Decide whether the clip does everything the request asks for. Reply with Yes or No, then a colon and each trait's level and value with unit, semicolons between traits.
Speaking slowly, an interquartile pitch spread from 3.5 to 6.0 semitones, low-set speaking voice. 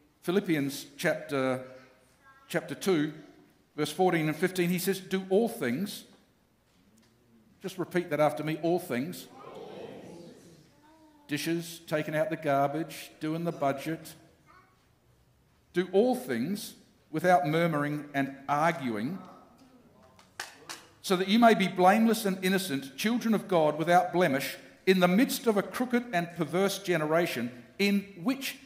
No: slow, 125 wpm; average, 4.7 semitones; medium, 175 Hz